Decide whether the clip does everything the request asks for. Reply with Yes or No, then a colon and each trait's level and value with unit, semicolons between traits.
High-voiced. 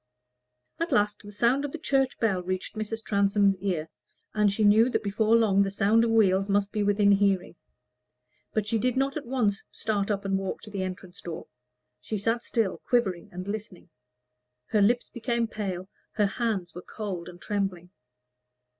Yes: high, 205 Hz